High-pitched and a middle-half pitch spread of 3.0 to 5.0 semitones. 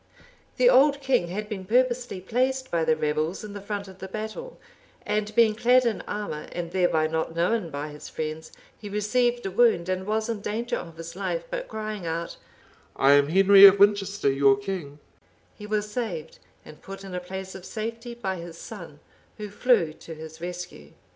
Yes: high, 195 Hz; average, 4.7 semitones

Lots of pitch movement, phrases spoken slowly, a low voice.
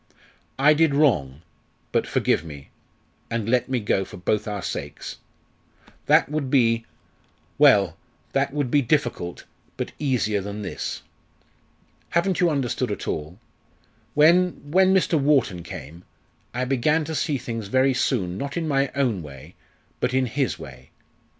No: wide, 6.3 semitones; average, 145 wpm; low, 130 Hz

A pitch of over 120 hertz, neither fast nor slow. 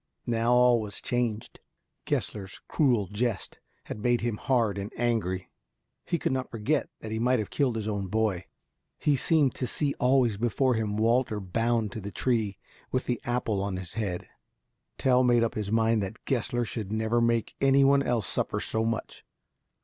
No: low, 115 Hz; average, 180 wpm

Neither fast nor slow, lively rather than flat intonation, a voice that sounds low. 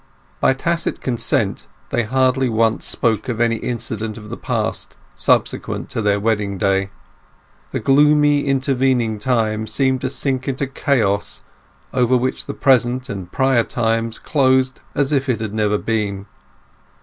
No: average, 145 wpm; average, 3.3 semitones; low, 120 Hz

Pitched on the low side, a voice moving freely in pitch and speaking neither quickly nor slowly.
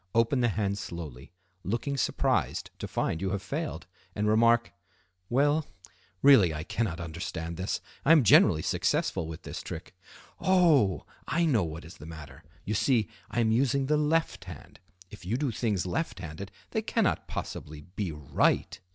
Yes: low, 105 Hz; wide, 7.9 semitones; average, 160 wpm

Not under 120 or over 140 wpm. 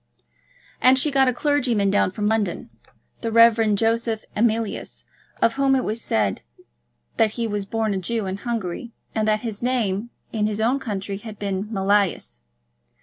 No: average, 165 wpm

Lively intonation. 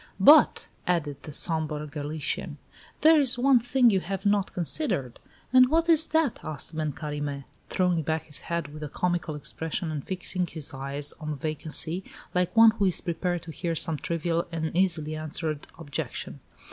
No: average, 3.9 semitones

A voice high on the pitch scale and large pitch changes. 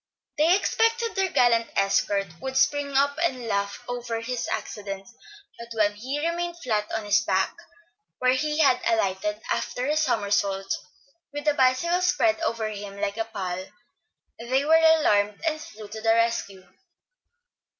Yes: high, 235 Hz; wide, 6.4 semitones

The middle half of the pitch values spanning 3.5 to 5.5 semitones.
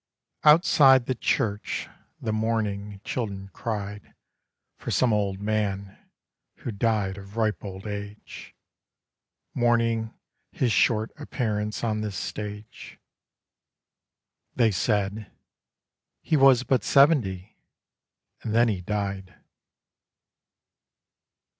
No: narrow, 2.6 semitones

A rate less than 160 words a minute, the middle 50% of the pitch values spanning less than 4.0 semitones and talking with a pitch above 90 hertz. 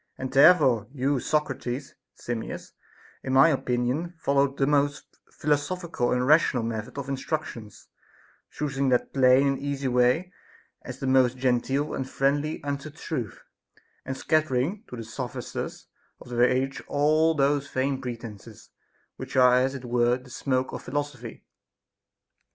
Yes: average, 140 wpm; narrow, 2.5 semitones; low, 135 Hz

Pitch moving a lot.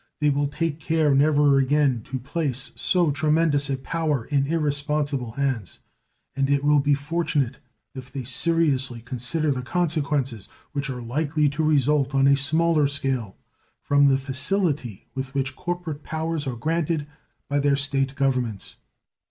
No: narrow, 2.4 semitones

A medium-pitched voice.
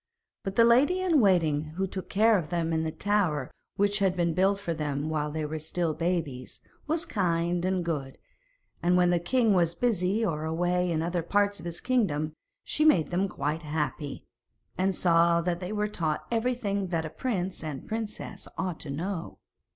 Yes: medium, 175 Hz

